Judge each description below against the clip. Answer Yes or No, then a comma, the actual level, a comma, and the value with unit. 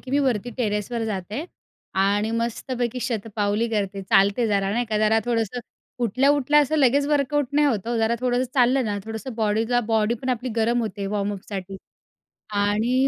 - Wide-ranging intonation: No, average, 3.4 semitones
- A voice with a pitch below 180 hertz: No, high, 230 Hz